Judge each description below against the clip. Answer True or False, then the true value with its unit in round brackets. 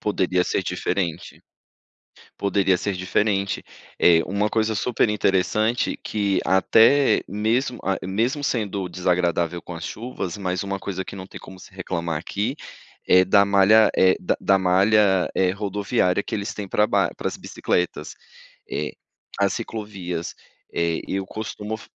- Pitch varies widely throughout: False (2.6 semitones)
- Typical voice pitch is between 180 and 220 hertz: False (100 Hz)